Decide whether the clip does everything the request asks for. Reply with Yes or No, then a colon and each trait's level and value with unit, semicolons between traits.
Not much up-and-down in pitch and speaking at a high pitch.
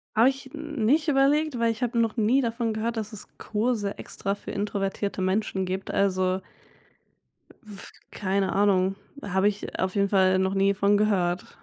No: average, 3.2 semitones; high, 205 Hz